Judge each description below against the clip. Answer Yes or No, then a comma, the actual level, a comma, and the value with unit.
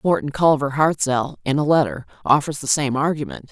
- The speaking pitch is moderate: Yes, medium, 145 Hz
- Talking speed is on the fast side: No, average, 170 wpm